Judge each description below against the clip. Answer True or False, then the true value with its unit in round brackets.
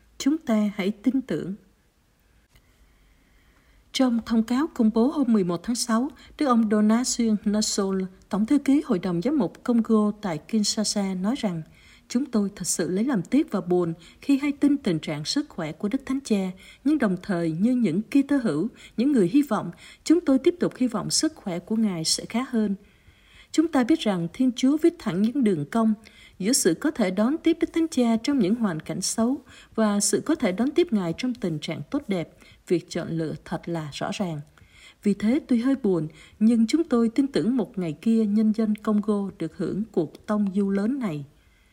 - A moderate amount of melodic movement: False (5.7 semitones)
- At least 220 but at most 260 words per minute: False (205 wpm)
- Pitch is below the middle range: False (215 Hz)